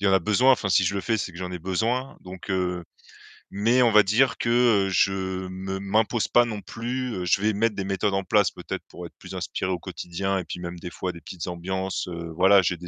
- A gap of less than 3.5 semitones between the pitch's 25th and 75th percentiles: Yes, average, 2.9 semitones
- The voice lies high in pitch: No, very low, 95 Hz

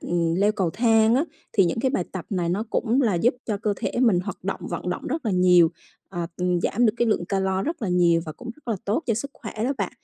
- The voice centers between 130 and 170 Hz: No, high, 205 Hz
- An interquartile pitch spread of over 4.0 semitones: Yes, average, 4.8 semitones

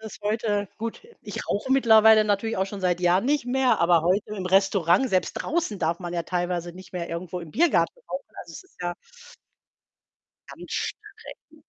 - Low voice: No, high, 195 Hz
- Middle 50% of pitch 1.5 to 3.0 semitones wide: No, average, 4.5 semitones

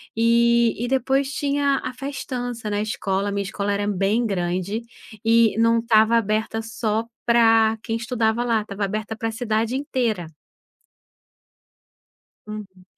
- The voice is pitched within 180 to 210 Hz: No, high, 225 Hz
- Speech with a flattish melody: Yes, narrow, 2.1 semitones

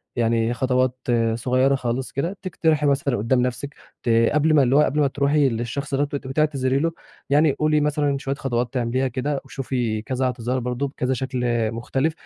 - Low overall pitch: Yes, low, 130 Hz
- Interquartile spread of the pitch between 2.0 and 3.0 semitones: Yes, narrow, 2.6 semitones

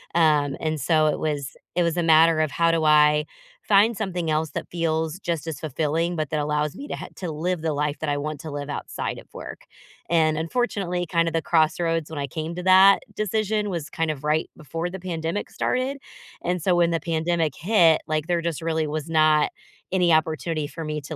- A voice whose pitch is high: No, medium, 160 Hz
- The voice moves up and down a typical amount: No, narrow, 2.1 semitones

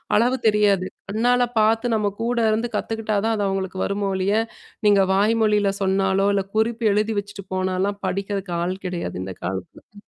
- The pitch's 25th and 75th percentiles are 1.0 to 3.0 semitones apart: Yes, narrow, 2.4 semitones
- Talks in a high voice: Yes, high, 205 Hz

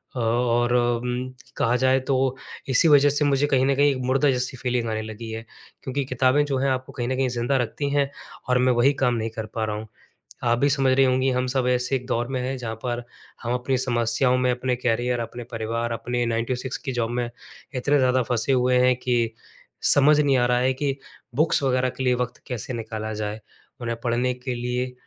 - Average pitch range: No, narrow, 1.7 semitones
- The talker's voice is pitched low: Yes, low, 125 Hz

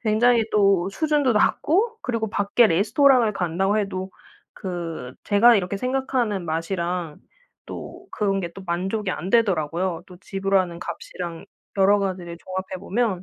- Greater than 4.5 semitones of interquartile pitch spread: No, average, 3.9 semitones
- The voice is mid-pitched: No, high, 195 Hz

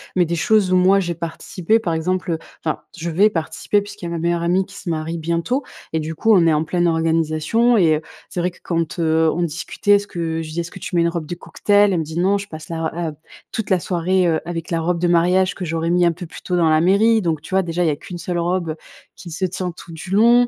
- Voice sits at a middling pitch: Yes, medium, 170 Hz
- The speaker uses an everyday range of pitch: No, narrow, 2.3 semitones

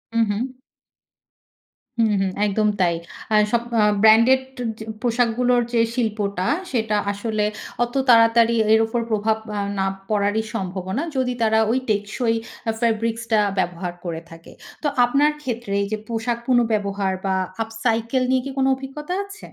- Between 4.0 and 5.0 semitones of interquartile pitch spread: No, average, 2.9 semitones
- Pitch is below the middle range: No, high, 225 Hz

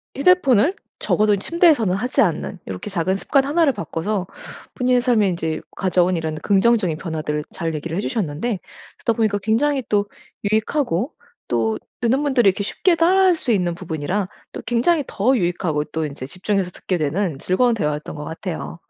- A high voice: Yes, high, 200 Hz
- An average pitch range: No, wide, 6.9 semitones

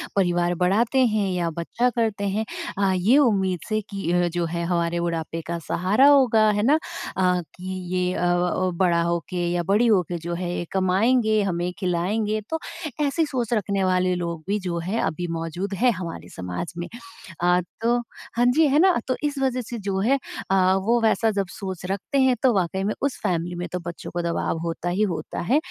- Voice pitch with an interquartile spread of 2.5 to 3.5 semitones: No, average, 4.4 semitones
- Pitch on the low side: No, high, 190 Hz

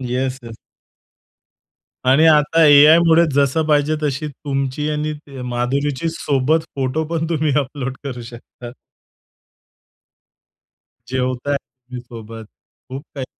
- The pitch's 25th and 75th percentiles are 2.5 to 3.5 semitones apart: Yes, average, 3.0 semitones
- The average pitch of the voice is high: No, medium, 140 Hz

